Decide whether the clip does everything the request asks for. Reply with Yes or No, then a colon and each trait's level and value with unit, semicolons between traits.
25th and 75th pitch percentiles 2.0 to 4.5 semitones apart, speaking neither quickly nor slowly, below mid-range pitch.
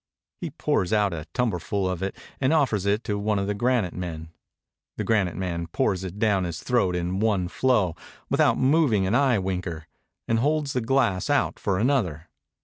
No: average, 5.0 semitones; average, 185 wpm; low, 100 Hz